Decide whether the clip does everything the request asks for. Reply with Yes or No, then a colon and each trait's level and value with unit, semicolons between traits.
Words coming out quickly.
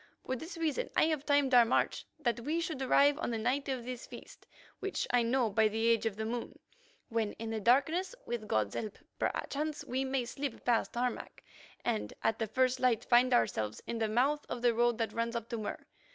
Yes: fast, 215 wpm